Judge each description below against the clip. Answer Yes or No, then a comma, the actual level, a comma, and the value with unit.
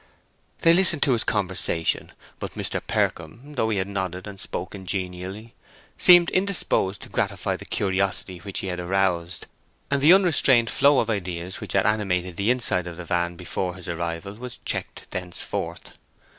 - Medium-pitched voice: No, very low, 95 Hz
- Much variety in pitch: No, average, 4.8 semitones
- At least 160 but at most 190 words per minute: Yes, average, 165 wpm